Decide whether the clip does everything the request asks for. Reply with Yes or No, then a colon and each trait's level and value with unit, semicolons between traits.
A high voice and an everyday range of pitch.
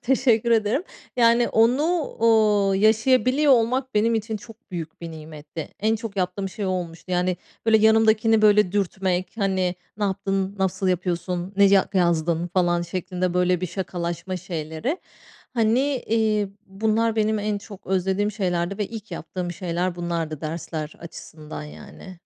Yes: high, 195 Hz; average, 3.9 semitones